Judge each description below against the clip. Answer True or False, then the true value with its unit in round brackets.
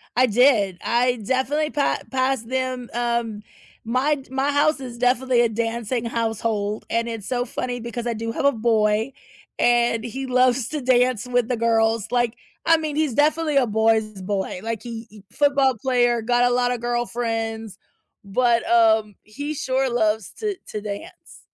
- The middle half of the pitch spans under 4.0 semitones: True (2.5 semitones)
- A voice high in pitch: True (240 Hz)